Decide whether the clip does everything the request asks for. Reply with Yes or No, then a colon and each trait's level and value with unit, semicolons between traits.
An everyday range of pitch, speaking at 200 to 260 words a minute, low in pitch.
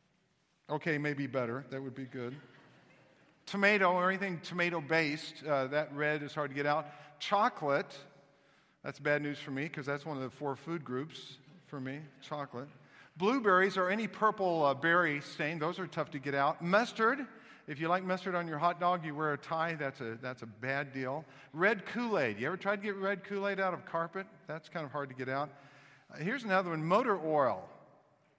No: average, 4.4 semitones; fast, 205 wpm; medium, 155 Hz